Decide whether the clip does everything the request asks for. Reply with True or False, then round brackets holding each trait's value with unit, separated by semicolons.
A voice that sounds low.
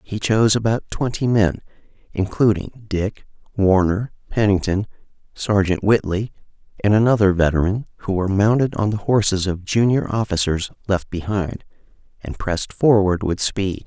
True (100 Hz)